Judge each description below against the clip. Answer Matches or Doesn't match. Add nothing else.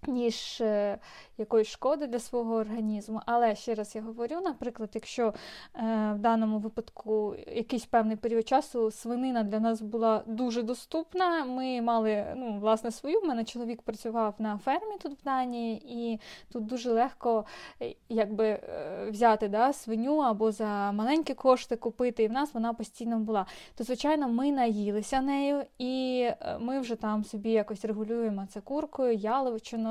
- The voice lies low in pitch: Doesn't match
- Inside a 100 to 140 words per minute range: Doesn't match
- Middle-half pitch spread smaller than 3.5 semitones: Matches